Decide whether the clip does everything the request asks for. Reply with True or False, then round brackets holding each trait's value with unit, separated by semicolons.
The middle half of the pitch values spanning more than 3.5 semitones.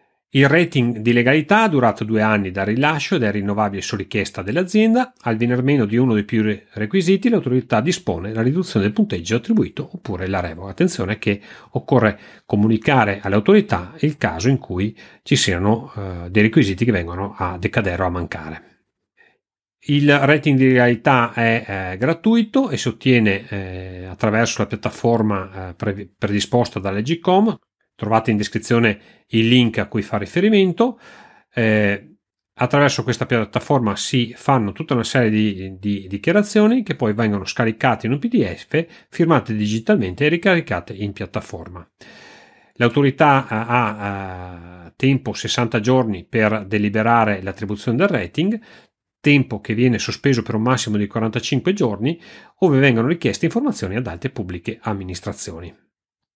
True (5.3 semitones)